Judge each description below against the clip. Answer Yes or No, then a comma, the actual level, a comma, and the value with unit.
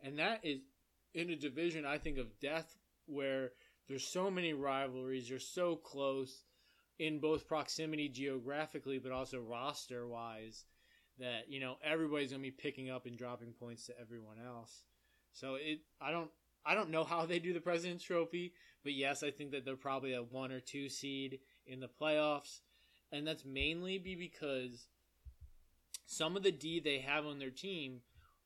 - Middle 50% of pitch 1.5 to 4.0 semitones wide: Yes, average, 3.5 semitones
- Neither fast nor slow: Yes, average, 170 wpm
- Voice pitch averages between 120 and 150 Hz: Yes, medium, 140 Hz